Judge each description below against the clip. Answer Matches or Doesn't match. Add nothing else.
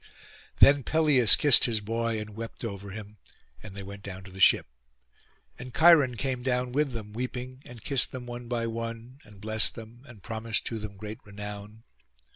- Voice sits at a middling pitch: Doesn't match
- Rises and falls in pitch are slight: Doesn't match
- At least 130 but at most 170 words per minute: Doesn't match